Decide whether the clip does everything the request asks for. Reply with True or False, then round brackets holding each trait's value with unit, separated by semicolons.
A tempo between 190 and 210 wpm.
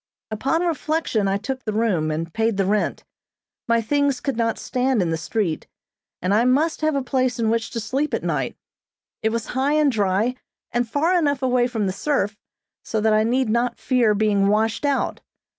True (195 wpm)